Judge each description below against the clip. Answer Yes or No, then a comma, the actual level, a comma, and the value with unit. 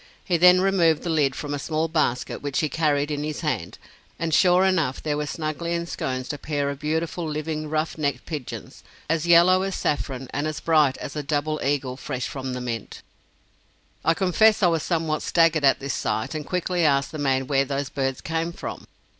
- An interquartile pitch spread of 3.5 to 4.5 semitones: No, average, 2.8 semitones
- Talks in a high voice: No, medium, 155 Hz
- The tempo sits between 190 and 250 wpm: Yes, average, 200 wpm